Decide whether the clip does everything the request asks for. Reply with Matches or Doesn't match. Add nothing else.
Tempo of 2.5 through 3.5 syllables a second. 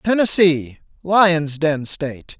Matches